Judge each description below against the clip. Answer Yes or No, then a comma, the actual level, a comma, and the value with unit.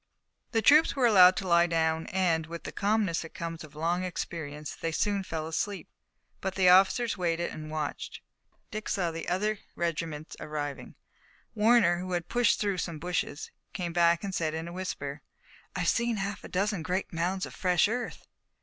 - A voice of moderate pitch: Yes, medium, 175 Hz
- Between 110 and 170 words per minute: No, average, 180 wpm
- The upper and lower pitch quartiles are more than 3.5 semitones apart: No, average, 3.2 semitones